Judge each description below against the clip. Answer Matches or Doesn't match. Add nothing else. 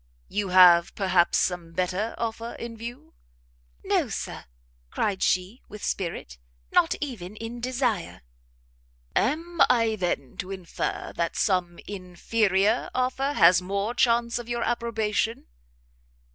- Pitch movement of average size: Matches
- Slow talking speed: Matches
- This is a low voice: Doesn't match